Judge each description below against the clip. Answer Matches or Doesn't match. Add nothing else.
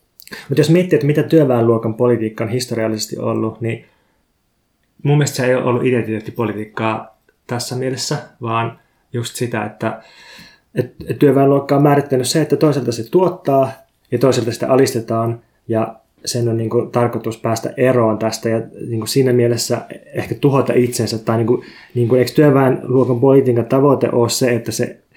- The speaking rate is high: Matches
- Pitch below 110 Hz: Doesn't match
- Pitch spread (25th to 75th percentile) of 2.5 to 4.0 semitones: Matches